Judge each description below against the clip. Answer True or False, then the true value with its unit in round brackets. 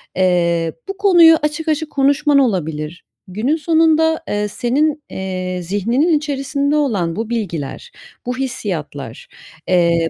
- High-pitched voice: True (240 Hz)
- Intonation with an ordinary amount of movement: False (9.0 semitones)